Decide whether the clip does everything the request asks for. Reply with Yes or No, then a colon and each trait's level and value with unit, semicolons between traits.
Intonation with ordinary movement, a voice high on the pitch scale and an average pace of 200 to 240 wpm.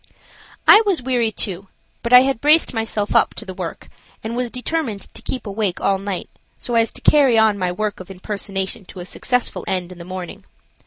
Yes: average, 4.6 semitones; high, 215 Hz; fast, 205 wpm